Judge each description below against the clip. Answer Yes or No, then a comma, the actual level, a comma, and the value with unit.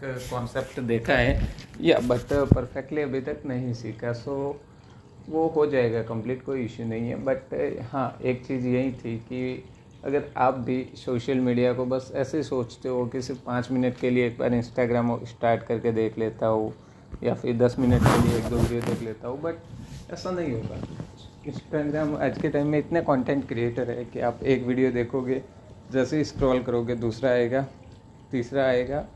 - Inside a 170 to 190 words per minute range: Yes, average, 185 wpm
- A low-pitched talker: Yes, low, 125 Hz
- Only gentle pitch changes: Yes, narrow, 2.2 semitones